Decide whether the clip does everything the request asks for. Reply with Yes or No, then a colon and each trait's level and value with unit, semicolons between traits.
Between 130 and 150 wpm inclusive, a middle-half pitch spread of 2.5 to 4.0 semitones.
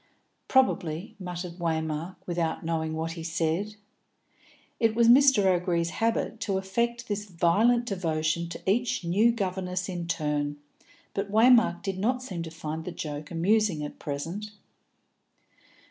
No: slow, 135 wpm; average, 4.5 semitones